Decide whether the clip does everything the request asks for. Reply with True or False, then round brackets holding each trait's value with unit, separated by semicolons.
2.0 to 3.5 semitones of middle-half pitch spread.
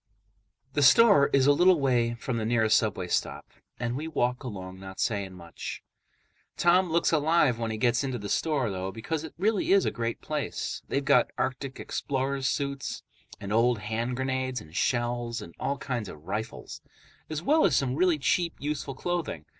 False (4.9 semitones)